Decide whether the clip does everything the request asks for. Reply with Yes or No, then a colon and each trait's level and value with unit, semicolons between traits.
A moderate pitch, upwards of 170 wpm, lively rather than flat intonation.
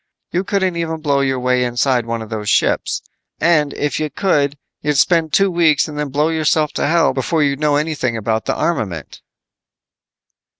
No: medium, 150 Hz; average, 180 wpm; average, 4.2 semitones